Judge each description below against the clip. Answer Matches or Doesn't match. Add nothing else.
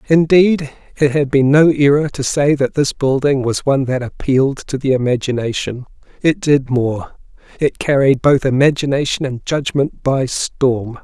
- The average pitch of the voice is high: Doesn't match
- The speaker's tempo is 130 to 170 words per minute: Matches